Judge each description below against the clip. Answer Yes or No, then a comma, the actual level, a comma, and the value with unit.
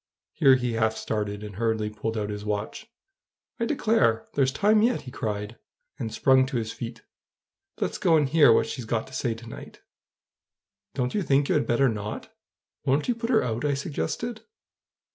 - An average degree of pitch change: Yes, average, 4.6 semitones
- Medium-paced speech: Yes, average, 185 wpm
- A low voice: Yes, low, 120 Hz